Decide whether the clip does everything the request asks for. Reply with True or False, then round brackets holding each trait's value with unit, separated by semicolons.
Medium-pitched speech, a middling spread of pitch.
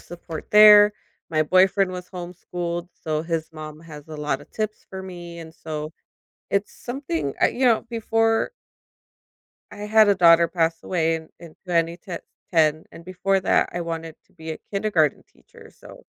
True (170 Hz; 3.3 semitones)